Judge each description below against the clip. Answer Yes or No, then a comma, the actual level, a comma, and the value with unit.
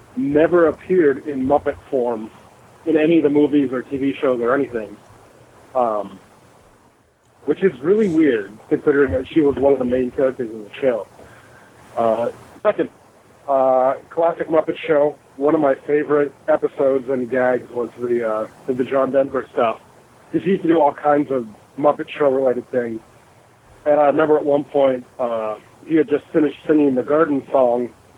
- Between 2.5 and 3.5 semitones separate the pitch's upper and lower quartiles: Yes, average, 3.1 semitones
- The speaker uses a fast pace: No, average, 170 wpm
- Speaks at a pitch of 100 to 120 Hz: No, medium, 140 Hz